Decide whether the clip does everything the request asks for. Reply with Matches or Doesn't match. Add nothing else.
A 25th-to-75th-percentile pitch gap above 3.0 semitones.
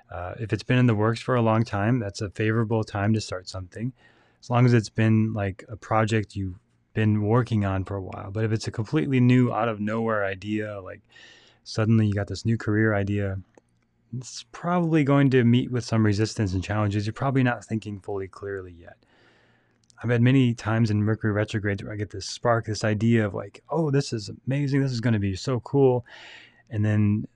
Doesn't match